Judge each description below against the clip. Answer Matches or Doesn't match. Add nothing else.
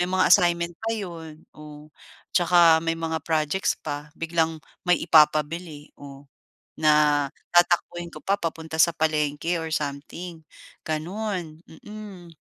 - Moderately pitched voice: Matches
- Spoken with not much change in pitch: Matches